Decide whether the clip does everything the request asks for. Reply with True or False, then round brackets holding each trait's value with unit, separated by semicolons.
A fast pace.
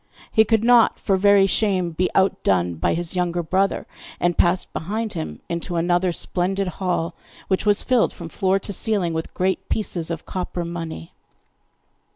False (165 wpm)